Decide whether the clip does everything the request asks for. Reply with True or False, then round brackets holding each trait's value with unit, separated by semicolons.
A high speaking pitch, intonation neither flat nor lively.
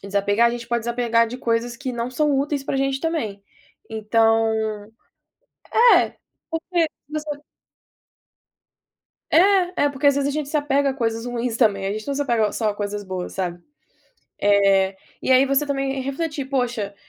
True (245 Hz; 4.3 semitones)